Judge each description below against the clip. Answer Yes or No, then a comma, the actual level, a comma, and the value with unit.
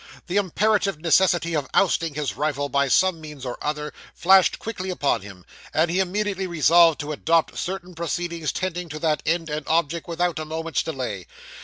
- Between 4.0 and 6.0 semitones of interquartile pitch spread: No, average, 3.0 semitones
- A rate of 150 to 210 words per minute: Yes, average, 175 wpm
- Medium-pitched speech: Yes, medium, 165 Hz